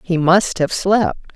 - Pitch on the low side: No, medium, 180 Hz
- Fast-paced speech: No, average, 175 wpm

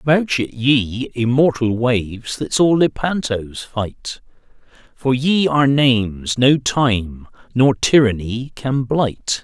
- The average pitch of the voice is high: No, low, 125 Hz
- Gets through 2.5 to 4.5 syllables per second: Yes, 3.4 syllables/s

